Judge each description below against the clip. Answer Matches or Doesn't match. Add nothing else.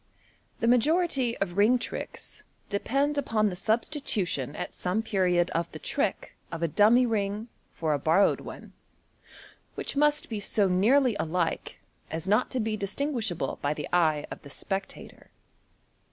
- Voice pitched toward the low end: Doesn't match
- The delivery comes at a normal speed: Matches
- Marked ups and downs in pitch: Matches